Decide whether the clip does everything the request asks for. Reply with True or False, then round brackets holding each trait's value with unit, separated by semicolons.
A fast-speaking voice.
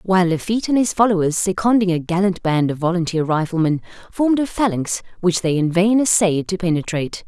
False (180 wpm)